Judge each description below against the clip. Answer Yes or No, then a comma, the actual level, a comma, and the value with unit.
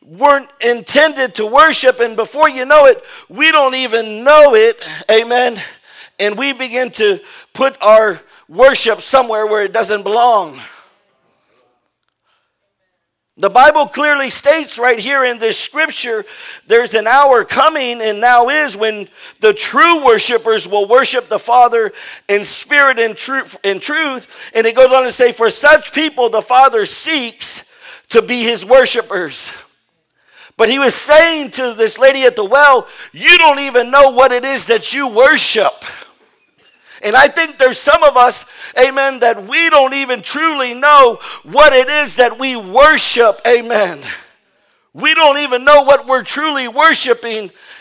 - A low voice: No, very high, 255 Hz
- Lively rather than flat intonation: No, average, 4.2 semitones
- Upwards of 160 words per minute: No, average, 150 wpm